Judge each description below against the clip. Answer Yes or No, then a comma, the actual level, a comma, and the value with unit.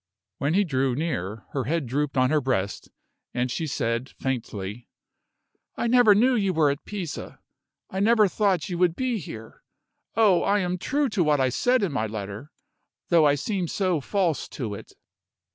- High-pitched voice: No, medium, 155 Hz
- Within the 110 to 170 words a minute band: No, average, 180 wpm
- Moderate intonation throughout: No, wide, 7.5 semitones